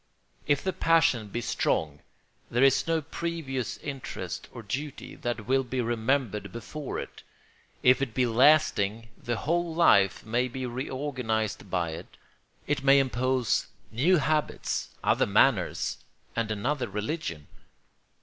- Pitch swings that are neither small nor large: Yes, average, 4.5 semitones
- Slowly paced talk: Yes, slow, 130 wpm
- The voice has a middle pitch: No, low, 125 Hz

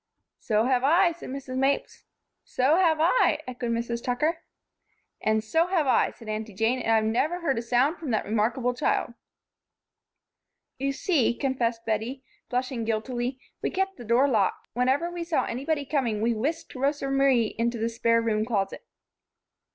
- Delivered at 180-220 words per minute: No, average, 165 wpm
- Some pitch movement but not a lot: Yes, average, 3.6 semitones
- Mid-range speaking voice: No, very high, 250 Hz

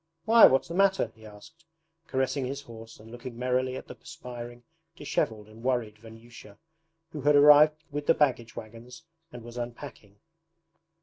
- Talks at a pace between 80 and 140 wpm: No, average, 160 wpm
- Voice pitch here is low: Yes, low, 125 Hz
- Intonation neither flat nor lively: Yes, average, 4.1 semitones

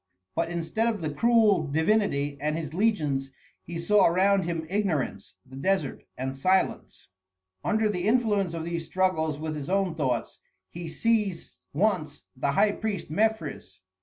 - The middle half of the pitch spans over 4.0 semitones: Yes, average, 5.1 semitones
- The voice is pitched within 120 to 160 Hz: No, medium, 170 Hz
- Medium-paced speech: Yes, average, 150 wpm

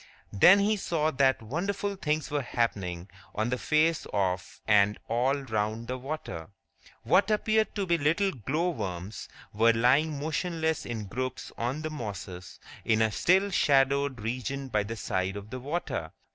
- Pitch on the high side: No, low, 130 Hz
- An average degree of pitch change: No, wide, 6.6 semitones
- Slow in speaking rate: No, average, 160 wpm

